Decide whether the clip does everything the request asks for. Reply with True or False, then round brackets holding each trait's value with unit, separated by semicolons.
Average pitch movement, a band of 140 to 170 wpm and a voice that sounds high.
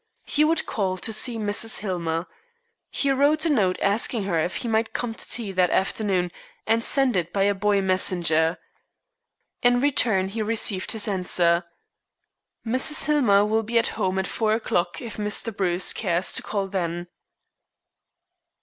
True (3.7 semitones; 160 wpm; 205 Hz)